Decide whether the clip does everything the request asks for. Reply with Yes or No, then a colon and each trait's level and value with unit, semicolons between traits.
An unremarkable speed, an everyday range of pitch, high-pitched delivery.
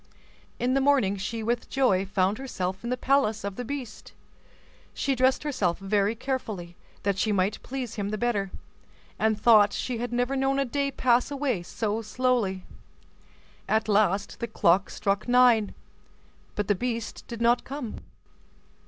Yes: average, 160 wpm; average, 4.0 semitones; high, 225 Hz